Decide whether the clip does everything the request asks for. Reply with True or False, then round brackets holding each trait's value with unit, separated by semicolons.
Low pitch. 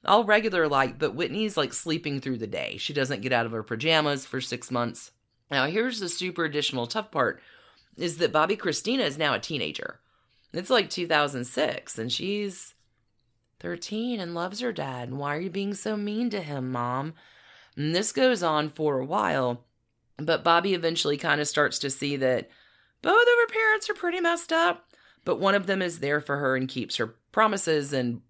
False (155 Hz)